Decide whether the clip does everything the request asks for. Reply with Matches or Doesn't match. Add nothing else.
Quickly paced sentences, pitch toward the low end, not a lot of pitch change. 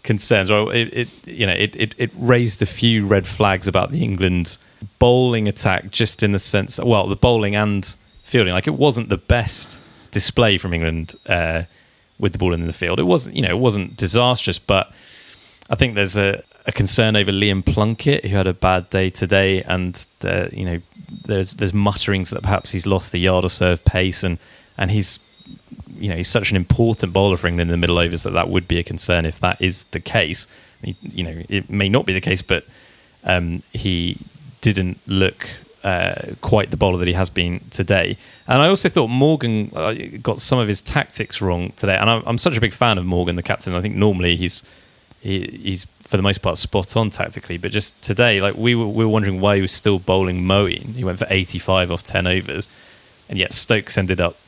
Doesn't match